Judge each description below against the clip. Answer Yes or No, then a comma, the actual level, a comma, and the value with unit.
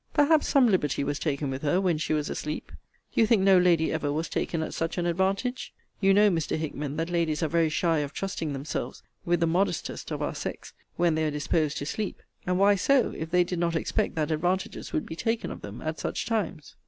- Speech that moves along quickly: Yes, fast, 230 wpm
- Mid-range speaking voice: Yes, medium, 165 Hz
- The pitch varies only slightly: No, average, 3.7 semitones